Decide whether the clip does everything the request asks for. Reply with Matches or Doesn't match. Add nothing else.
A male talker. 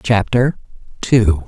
Matches